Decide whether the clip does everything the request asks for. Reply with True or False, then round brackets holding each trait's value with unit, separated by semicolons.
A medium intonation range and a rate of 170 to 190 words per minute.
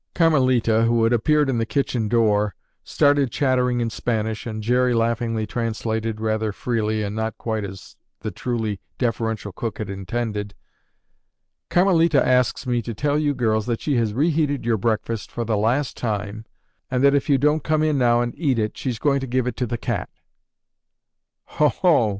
True (3.5 semitones; 175 wpm)